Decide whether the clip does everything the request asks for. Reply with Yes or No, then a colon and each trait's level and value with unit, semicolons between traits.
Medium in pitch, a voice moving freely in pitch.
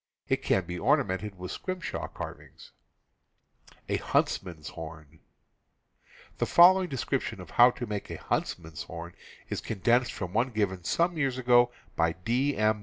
No: low, 110 Hz; wide, 6.2 semitones